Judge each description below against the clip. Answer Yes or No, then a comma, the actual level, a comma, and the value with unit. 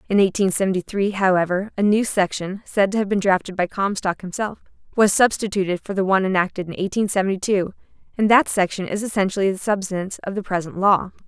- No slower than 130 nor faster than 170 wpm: No, average, 195 wpm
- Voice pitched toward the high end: Yes, high, 195 Hz